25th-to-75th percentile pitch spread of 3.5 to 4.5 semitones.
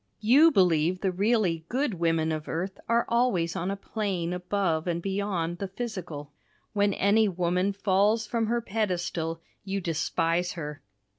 Yes: average, 3.8 semitones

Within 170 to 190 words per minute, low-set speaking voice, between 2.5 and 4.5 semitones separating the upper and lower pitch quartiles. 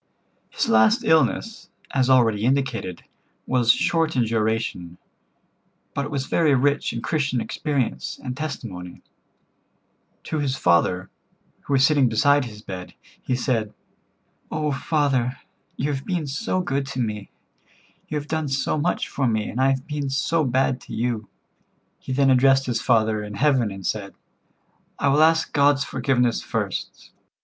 No: average, 155 wpm; low, 130 Hz; average, 4.1 semitones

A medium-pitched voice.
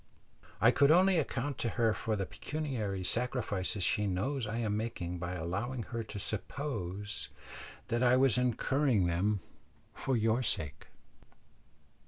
No: low, 115 Hz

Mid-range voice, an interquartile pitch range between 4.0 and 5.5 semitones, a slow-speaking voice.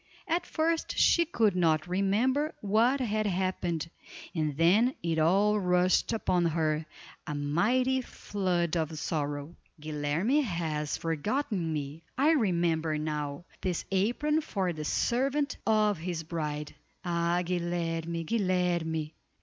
Yes: medium, 175 Hz; average, 5.1 semitones; slow, 120 wpm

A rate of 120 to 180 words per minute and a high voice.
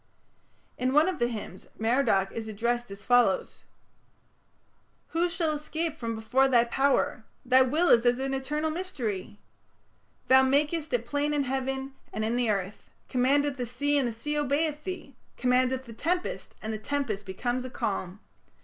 Yes: average, 165 wpm; very high, 260 Hz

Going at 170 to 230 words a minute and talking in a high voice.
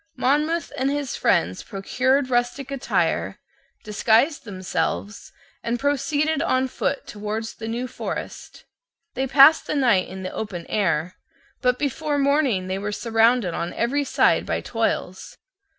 No: slow, 135 wpm; high, 245 Hz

